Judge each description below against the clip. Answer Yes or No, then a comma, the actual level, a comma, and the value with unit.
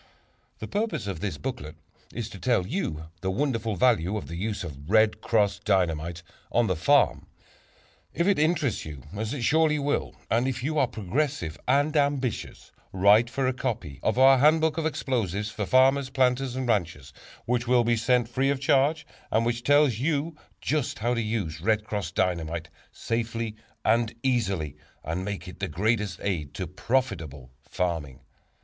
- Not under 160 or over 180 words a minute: Yes, average, 170 wpm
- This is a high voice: No, low, 115 Hz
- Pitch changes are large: Yes, wide, 6.3 semitones